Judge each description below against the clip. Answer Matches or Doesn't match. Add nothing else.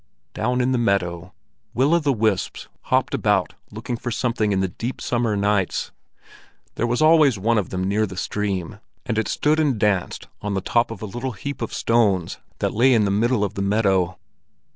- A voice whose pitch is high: Doesn't match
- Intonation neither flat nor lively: Matches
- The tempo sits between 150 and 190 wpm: Doesn't match